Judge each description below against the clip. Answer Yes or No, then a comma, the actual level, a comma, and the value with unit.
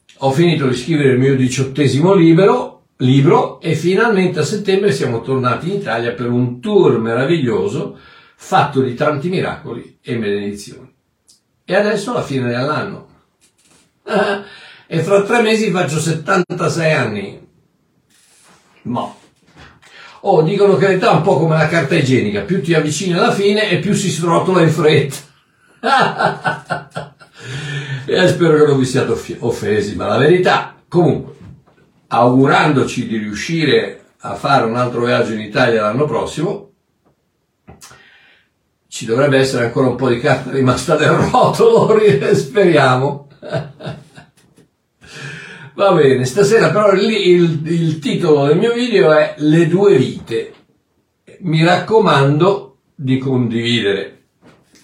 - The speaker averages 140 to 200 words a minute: No, average, 125 wpm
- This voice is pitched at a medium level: Yes, medium, 155 Hz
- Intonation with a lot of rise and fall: Yes, wide, 6.1 semitones